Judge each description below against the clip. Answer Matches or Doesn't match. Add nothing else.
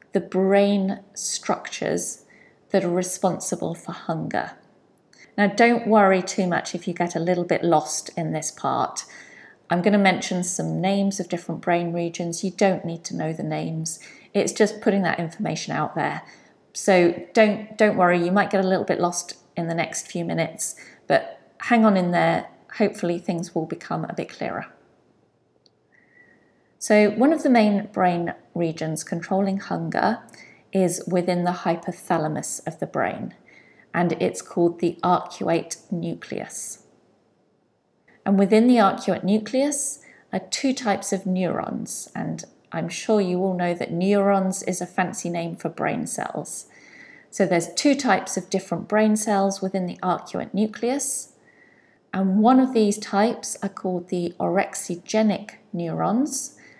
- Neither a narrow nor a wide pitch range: Matches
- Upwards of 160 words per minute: Doesn't match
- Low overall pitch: Doesn't match